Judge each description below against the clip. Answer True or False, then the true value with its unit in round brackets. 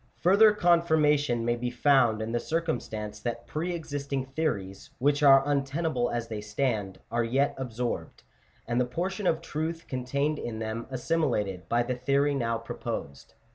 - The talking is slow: False (165 wpm)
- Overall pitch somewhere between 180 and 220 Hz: False (130 Hz)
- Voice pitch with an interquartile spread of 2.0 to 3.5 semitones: False (4.5 semitones)